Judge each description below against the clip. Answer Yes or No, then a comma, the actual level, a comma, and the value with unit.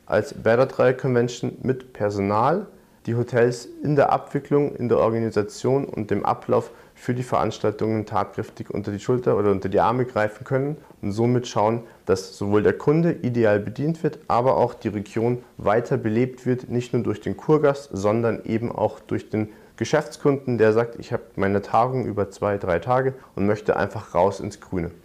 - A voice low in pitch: Yes, low, 120 Hz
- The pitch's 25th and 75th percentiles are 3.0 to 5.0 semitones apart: Yes, average, 3.7 semitones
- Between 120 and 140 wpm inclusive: No, average, 175 wpm